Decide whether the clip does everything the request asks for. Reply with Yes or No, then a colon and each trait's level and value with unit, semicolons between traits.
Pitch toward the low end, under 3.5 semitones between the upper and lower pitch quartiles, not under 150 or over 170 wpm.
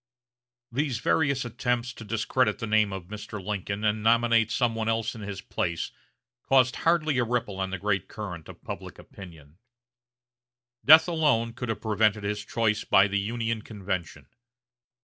Yes: low, 110 Hz; average, 3.0 semitones; average, 160 wpm